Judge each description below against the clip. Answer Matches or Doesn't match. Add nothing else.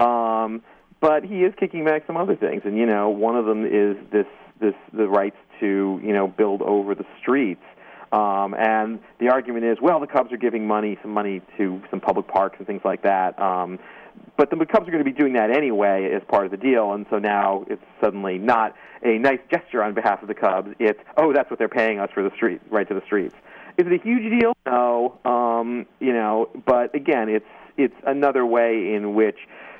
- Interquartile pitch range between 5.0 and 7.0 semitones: Matches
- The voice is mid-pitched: Doesn't match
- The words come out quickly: Matches